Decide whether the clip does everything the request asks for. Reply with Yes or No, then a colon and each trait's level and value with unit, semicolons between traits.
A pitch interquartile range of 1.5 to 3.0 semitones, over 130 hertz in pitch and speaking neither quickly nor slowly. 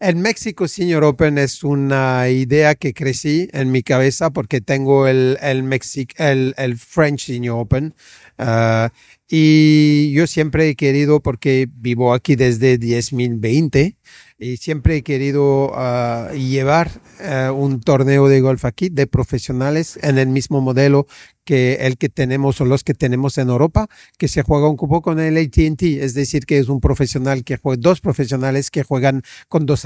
Yes: narrow, 2.5 semitones; medium, 140 Hz; average, 165 wpm